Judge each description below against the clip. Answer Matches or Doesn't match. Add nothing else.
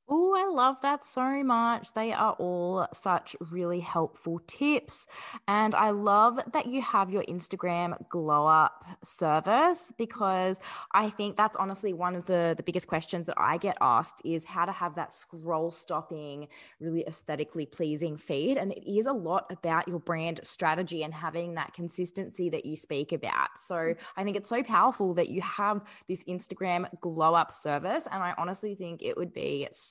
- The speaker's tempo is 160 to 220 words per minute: Matches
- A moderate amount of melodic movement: Matches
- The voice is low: Doesn't match